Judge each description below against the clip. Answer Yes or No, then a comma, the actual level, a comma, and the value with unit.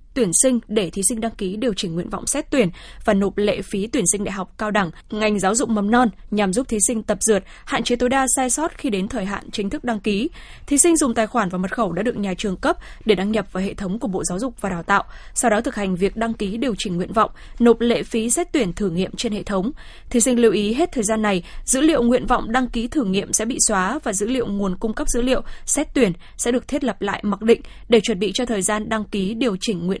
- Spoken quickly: Yes, fast, 285 wpm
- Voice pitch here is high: Yes, high, 220 Hz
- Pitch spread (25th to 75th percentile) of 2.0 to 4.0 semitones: Yes, average, 3.6 semitones